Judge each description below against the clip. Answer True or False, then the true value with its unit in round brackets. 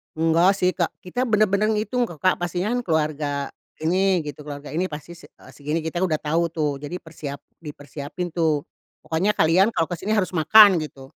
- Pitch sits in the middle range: True (165 Hz)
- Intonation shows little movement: False (3.7 semitones)